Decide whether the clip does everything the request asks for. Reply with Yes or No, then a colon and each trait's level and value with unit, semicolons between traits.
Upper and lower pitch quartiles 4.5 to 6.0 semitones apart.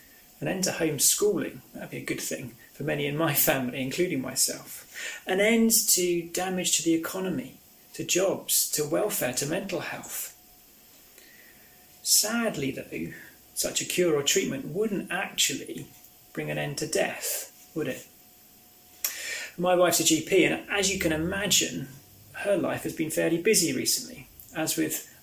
Yes: average, 4.9 semitones